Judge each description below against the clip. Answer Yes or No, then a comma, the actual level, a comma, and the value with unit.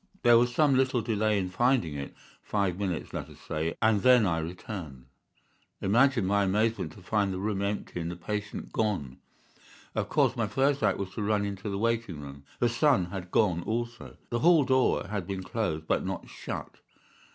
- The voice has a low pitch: Yes, low, 105 Hz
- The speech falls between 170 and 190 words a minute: Yes, average, 185 wpm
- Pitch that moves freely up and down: No, average, 4.4 semitones